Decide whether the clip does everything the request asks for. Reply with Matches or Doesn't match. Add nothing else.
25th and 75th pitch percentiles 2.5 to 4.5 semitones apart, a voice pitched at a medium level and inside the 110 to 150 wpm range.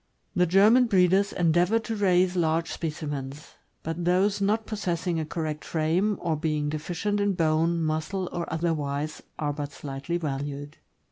Matches